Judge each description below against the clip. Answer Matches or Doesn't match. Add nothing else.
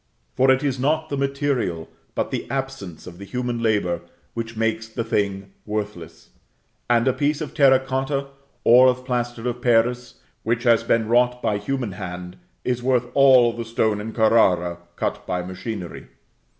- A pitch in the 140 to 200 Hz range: Doesn't match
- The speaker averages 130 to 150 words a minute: Doesn't match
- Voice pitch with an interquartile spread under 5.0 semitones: Matches